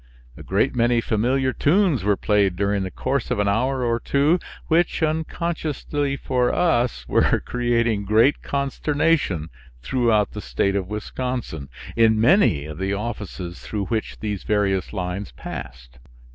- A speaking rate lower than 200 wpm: Yes, average, 145 wpm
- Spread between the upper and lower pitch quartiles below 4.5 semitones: No, wide, 5.4 semitones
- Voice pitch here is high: No, low, 115 Hz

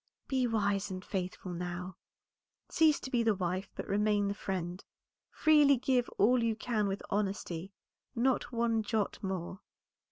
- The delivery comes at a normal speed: Yes, average, 150 wpm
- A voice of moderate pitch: No, high, 205 Hz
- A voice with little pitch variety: No, average, 3.9 semitones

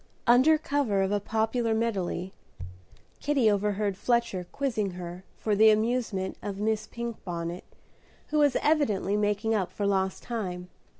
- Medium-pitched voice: No, high, 210 Hz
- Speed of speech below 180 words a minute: Yes, slow, 135 wpm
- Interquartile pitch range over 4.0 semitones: No, average, 3.6 semitones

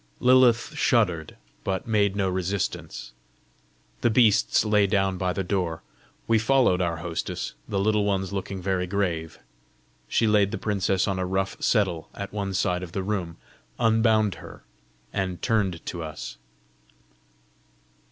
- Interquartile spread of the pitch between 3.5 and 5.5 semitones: No, average, 2.7 semitones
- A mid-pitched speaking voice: No, very low, 95 Hz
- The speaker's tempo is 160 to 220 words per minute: No, average, 140 wpm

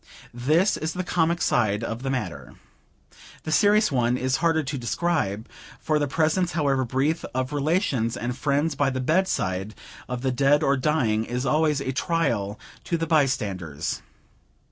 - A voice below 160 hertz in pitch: Yes, medium, 140 Hz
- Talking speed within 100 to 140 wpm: No, average, 160 wpm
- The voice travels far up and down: No, average, 4.6 semitones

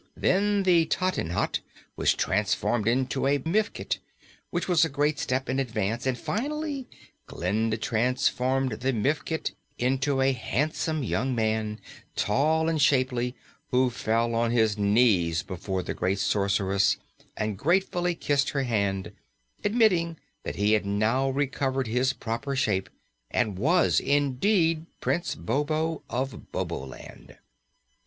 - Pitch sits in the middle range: No, low, 130 Hz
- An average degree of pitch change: No, wide, 6.1 semitones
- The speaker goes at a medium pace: No, slow, 125 wpm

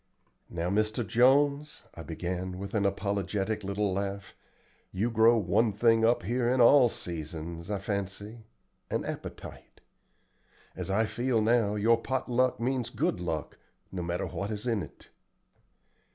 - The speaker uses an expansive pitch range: No, average, 3.7 semitones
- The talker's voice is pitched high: No, low, 105 Hz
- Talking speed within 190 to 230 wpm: No, average, 145 wpm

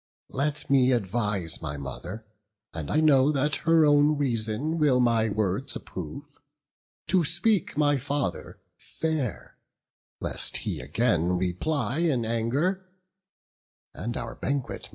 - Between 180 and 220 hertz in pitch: No, low, 130 Hz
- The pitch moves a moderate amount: No, wide, 5.7 semitones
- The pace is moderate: No, slow, 125 wpm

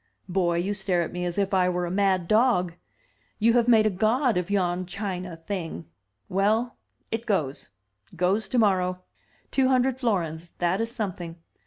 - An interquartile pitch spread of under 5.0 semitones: Yes, average, 3.7 semitones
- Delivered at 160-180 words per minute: Yes, average, 170 wpm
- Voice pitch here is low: No, high, 190 Hz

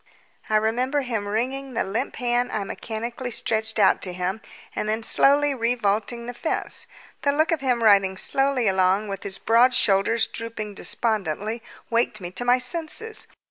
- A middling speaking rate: Yes, average, 165 wpm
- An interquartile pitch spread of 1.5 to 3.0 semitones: No, average, 3.4 semitones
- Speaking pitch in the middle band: No, high, 230 Hz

